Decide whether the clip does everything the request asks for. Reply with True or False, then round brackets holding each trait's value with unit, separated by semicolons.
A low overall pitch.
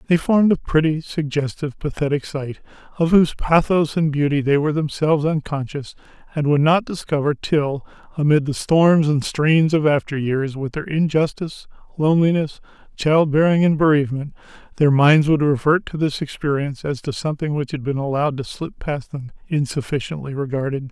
False (150 Hz)